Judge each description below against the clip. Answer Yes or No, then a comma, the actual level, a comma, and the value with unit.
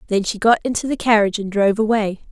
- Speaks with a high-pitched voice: Yes, high, 215 Hz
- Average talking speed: No, fast, 235 wpm